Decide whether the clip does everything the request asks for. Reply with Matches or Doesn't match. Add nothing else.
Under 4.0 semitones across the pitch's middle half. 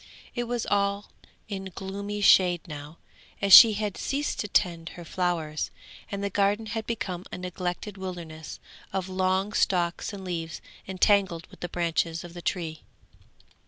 Matches